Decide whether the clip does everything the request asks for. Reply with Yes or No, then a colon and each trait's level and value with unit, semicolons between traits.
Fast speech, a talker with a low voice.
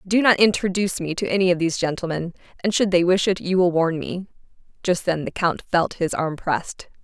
No: fast, 220 wpm; medium, 180 Hz